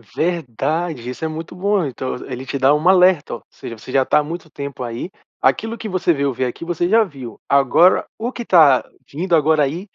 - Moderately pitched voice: Yes, medium, 155 Hz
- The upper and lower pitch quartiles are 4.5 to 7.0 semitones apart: Yes, average, 4.9 semitones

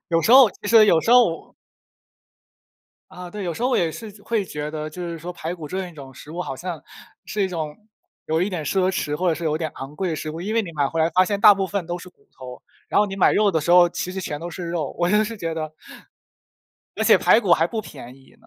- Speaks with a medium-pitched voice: Yes, medium, 175 Hz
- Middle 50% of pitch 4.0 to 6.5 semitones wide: No, average, 3.6 semitones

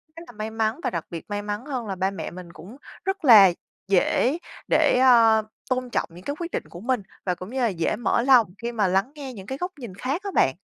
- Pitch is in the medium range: No, high, 225 Hz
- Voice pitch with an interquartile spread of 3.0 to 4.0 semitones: No, average, 5.3 semitones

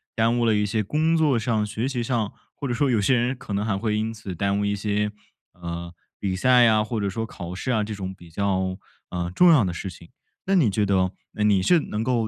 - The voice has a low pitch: Yes, low, 105 Hz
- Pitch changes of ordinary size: Yes, average, 3.6 semitones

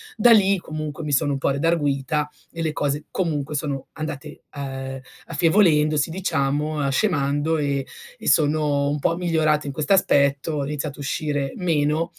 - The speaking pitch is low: No, medium, 150 Hz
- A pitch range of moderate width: No, narrow, 2.2 semitones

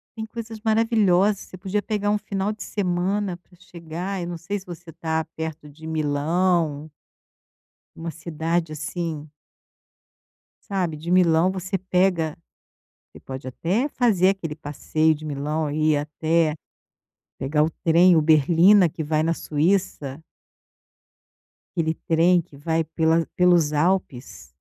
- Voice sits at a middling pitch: Yes, medium, 165 Hz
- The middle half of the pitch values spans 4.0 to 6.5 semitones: No, average, 3.1 semitones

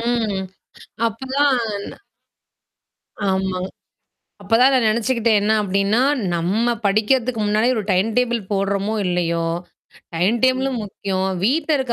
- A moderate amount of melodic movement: Yes, average, 3.8 semitones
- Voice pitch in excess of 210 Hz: Yes, high, 220 Hz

